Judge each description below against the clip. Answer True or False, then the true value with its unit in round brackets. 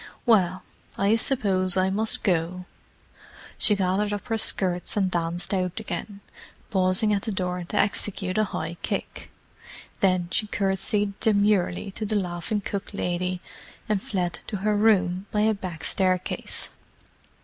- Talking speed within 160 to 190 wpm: False (145 wpm)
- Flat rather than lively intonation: True (2.3 semitones)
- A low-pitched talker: False (195 Hz)